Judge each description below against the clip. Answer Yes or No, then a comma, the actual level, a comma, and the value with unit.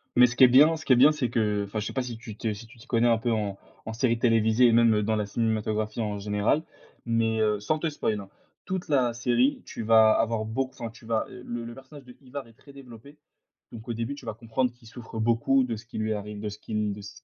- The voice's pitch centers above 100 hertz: Yes, low, 115 Hz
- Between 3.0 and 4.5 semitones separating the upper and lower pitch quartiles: No, narrow, 2.5 semitones